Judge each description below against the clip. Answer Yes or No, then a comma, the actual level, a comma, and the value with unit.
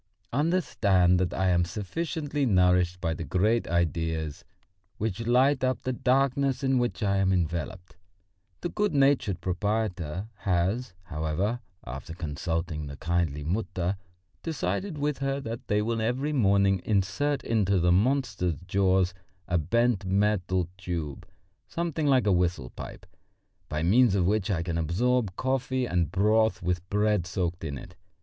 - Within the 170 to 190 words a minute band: No, average, 145 wpm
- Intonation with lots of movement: Yes, wide, 5.9 semitones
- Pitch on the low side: Yes, very low, 95 Hz